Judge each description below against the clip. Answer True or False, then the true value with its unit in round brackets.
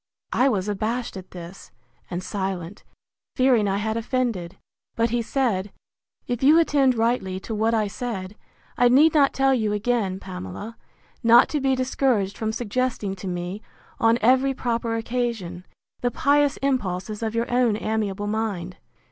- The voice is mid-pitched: False (225 Hz)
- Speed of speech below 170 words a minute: True (155 wpm)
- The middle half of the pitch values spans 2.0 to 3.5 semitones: False (4.4 semitones)